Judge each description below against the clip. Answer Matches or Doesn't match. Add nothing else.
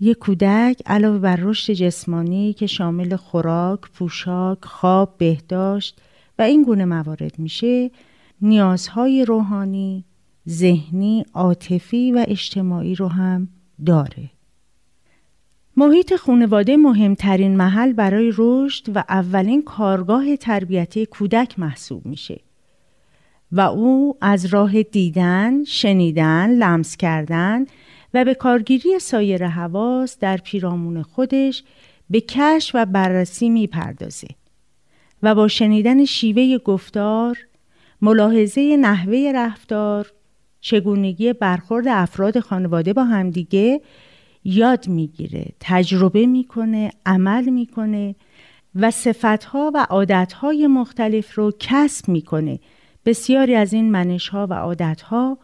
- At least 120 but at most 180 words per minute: Doesn't match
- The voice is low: Doesn't match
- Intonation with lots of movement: Doesn't match